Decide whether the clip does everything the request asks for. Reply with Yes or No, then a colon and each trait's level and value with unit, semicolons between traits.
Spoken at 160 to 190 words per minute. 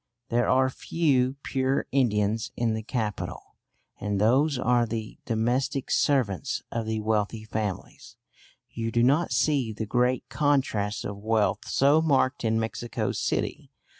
No: slow, 135 wpm